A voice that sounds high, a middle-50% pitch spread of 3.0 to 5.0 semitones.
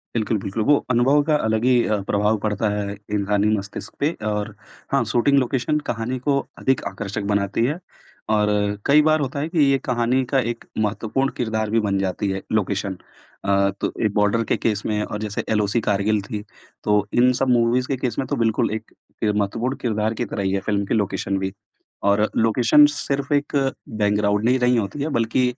No: low, 110 Hz; average, 3.6 semitones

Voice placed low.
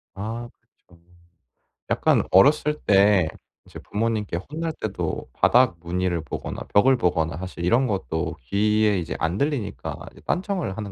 Yes: low, 100 Hz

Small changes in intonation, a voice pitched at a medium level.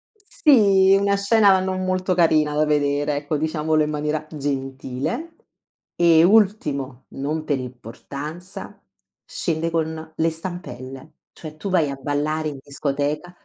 No: average, 4.1 semitones; medium, 155 Hz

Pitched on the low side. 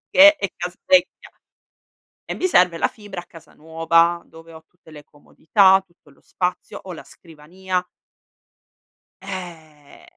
No: medium, 175 Hz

